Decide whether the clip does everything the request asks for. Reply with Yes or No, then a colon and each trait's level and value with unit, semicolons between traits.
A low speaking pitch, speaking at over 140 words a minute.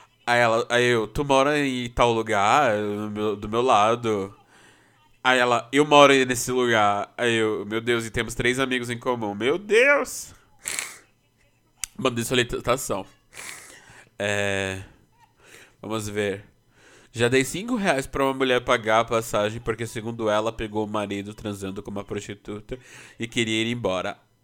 Yes: low, 115 Hz; average, 150 wpm